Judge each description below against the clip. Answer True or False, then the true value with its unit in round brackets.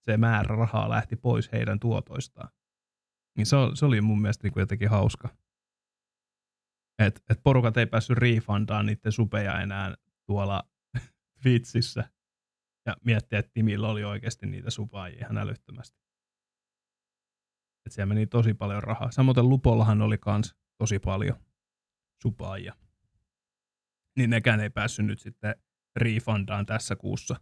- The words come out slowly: False (130 wpm)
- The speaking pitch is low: True (105 Hz)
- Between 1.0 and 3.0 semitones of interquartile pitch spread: True (2.5 semitones)